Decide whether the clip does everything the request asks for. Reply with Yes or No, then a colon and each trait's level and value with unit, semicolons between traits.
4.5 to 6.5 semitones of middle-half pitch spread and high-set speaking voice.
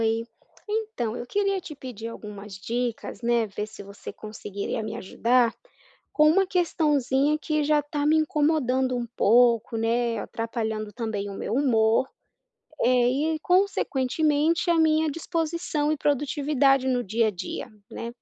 Yes: average, 5.1 semitones; very high, 255 Hz